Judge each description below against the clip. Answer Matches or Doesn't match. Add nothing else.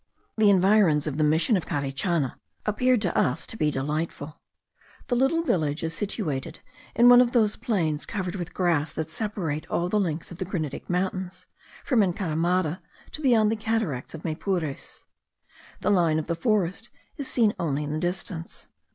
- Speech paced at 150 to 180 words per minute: Matches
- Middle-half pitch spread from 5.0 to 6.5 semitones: Matches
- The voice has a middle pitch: Matches